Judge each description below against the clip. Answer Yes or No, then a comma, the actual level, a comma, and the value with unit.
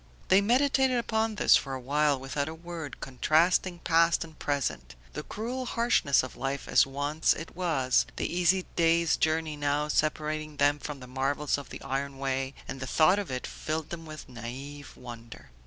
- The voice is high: No, medium, 150 Hz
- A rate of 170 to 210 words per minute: Yes, average, 180 wpm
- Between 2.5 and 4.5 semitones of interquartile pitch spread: Yes, average, 3.8 semitones